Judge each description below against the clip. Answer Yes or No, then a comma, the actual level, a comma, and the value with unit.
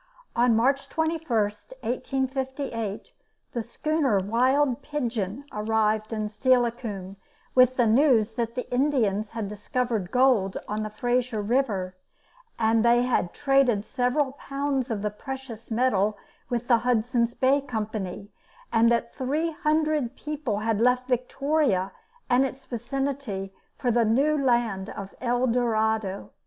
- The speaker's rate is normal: No, slow, 125 wpm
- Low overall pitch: No, high, 240 Hz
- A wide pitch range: No, average, 3.7 semitones